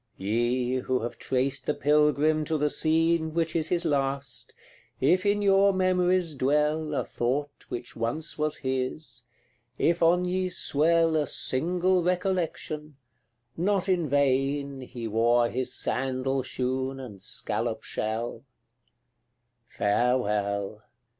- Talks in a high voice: No, medium, 145 Hz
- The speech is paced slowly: Yes, slow, 120 wpm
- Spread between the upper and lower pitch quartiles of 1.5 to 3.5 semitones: No, average, 4.6 semitones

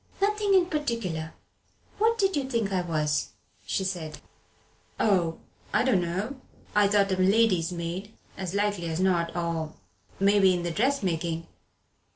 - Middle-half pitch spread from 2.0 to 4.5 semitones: No, average, 5.2 semitones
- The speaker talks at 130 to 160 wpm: Yes, average, 140 wpm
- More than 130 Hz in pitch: Yes, high, 190 Hz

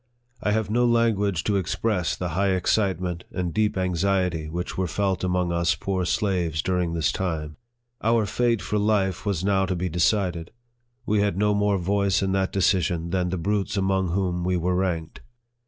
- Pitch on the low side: Yes, very low, 95 Hz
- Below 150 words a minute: No, average, 180 wpm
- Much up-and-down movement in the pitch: No, narrow, 2.5 semitones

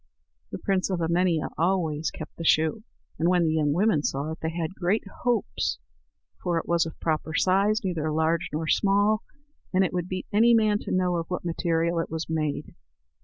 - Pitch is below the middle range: No, medium, 170 Hz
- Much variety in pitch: No, average, 2.9 semitones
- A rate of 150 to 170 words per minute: No, average, 195 wpm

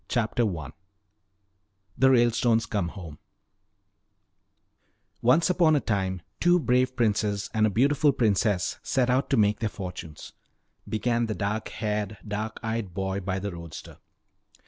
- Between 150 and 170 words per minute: No, average, 140 wpm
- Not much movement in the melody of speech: No, average, 3.8 semitones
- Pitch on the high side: No, low, 110 Hz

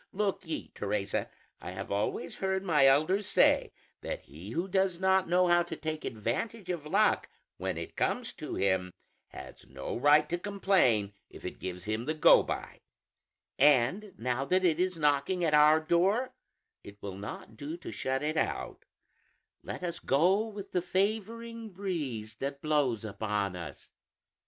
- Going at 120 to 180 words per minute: Yes, average, 165 wpm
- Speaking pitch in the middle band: Yes, medium, 155 Hz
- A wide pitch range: Yes, wide, 8.7 semitones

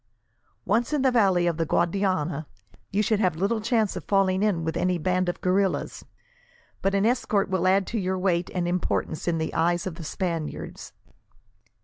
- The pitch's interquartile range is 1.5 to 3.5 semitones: Yes, narrow, 2.6 semitones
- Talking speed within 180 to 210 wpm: Yes, average, 185 wpm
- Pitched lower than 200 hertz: Yes, medium, 185 Hz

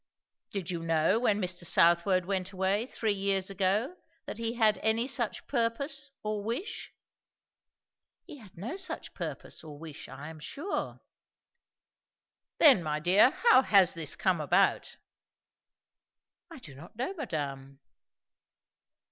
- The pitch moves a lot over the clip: Yes, wide, 6.0 semitones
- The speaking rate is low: Yes, slow, 130 wpm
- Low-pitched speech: No, high, 200 Hz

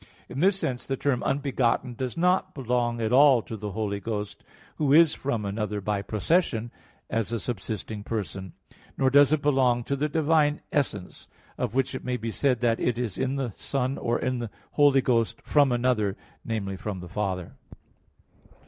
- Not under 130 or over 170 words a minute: No, average, 180 wpm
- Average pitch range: Yes, average, 4.3 semitones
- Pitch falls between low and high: No, low, 120 Hz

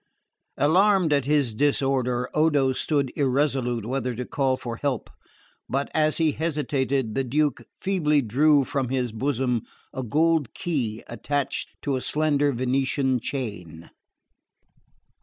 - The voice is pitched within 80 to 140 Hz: Yes, low, 135 Hz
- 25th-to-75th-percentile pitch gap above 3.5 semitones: No, average, 2.9 semitones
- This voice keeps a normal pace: No, slow, 125 wpm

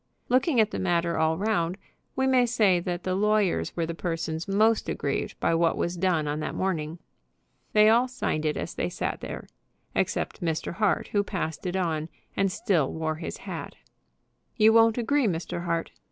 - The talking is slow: No, average, 180 wpm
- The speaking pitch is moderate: Yes, medium, 180 Hz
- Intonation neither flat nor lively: Yes, average, 4.7 semitones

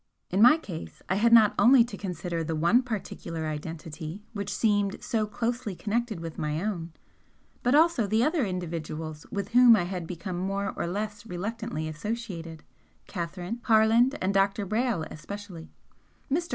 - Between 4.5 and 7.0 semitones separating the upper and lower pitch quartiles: Yes, average, 5.3 semitones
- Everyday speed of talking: Yes, average, 155 wpm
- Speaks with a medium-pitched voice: No, high, 200 Hz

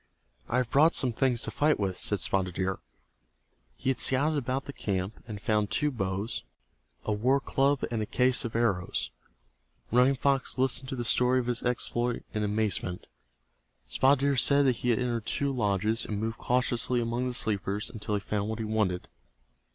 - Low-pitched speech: Yes, low, 120 Hz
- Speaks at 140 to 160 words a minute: No, average, 185 wpm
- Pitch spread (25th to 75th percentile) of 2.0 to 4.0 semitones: Yes, average, 3.7 semitones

